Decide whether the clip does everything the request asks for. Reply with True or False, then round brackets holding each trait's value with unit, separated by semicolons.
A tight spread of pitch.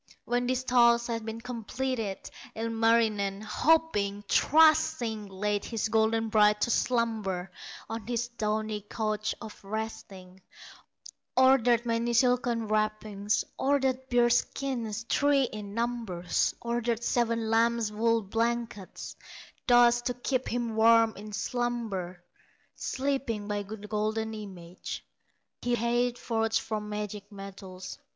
True (2.3 semitones)